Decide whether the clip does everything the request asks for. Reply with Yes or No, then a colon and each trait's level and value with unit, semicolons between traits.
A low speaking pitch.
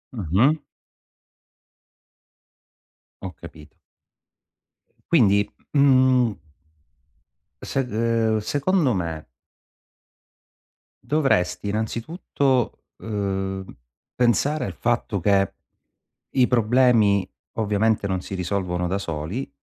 Yes: low, 110 Hz